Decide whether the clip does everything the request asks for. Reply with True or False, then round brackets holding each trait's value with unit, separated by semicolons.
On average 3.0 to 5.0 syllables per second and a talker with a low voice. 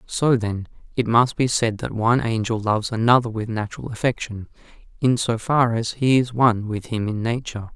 False (5.4 syllables/s; 115 Hz)